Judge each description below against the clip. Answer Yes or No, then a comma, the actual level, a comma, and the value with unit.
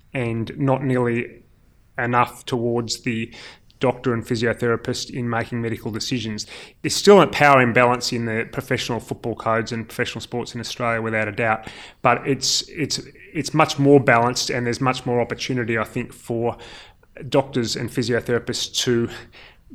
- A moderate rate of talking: Yes, average, 150 wpm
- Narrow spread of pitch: Yes, narrow, 1.7 semitones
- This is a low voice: Yes, low, 120 Hz